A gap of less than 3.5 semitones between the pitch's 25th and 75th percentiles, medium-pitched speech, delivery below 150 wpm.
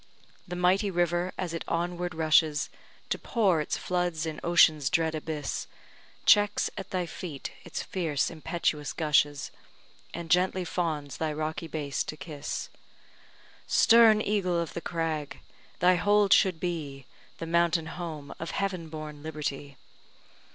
Yes: narrow, 2.6 semitones; medium, 165 Hz; slow, 135 wpm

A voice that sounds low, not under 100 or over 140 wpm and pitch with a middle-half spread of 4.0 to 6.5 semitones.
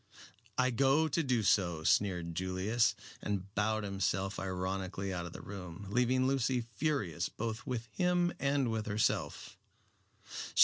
Yes: low, 105 Hz; slow, 135 wpm; average, 5.2 semitones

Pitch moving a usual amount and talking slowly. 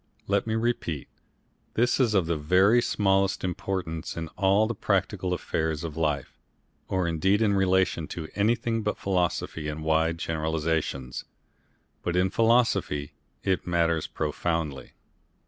Yes: average, 4.1 semitones; slow, 130 wpm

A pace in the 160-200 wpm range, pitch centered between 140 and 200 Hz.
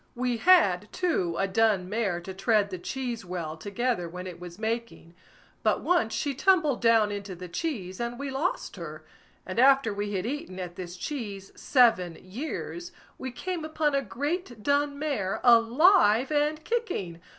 No: average, 165 wpm; high, 230 Hz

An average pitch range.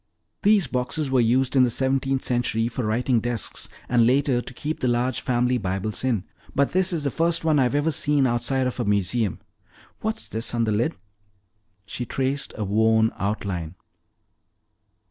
Yes: average, 3.3 semitones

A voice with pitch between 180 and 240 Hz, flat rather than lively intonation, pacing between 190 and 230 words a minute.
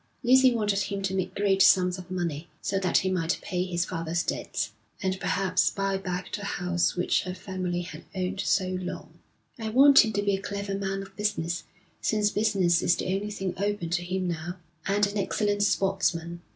Yes: high, 190 Hz; narrow, 2.2 semitones; average, 195 wpm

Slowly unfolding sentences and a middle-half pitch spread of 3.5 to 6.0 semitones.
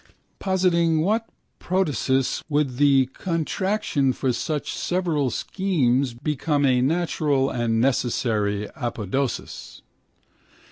Yes: slow, 90 wpm; average, 5.1 semitones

